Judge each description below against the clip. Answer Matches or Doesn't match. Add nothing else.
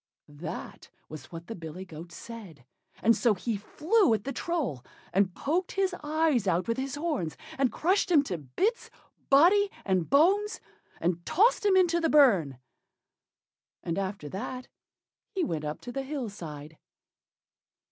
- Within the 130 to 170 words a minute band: Matches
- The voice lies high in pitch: Matches